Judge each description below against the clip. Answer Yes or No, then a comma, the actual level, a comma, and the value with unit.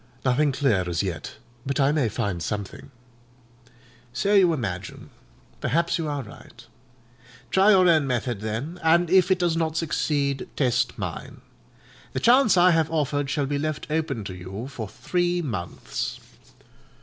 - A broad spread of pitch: Yes, wide, 6.6 semitones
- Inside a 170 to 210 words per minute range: No, average, 150 wpm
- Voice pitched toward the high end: No, medium, 145 Hz